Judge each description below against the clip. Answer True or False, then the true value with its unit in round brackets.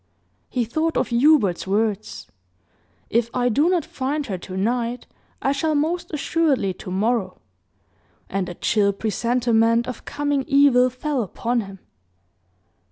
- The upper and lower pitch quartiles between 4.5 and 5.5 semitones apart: True (5.1 semitones)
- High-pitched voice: True (240 Hz)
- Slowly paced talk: True (130 wpm)